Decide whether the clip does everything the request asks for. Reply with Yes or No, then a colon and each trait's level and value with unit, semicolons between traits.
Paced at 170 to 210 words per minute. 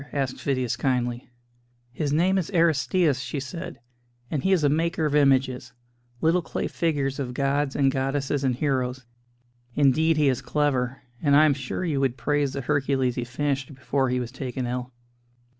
Yes: average, 175 wpm